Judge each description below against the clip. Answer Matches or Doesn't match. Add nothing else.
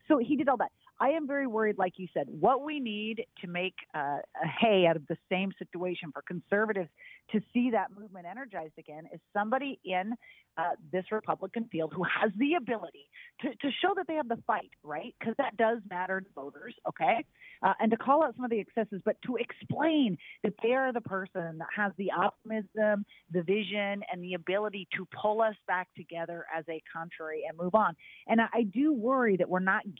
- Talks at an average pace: Doesn't match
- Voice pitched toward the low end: Doesn't match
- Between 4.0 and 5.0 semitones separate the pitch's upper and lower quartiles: Matches